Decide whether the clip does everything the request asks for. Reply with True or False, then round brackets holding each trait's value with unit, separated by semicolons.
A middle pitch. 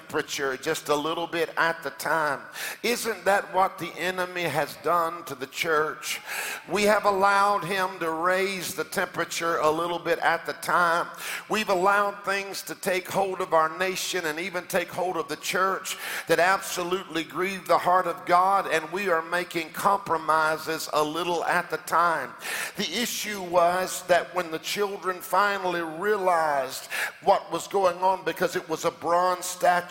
True (175 Hz)